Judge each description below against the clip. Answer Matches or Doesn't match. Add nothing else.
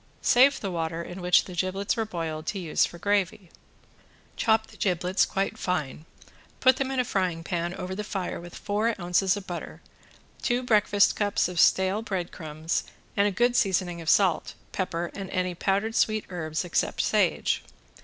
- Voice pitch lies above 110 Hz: Matches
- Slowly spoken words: Doesn't match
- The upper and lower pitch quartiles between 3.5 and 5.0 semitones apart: Doesn't match